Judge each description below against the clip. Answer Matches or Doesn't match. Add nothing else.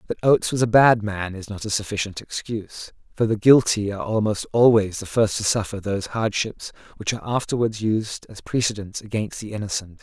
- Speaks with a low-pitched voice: Matches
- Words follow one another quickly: Doesn't match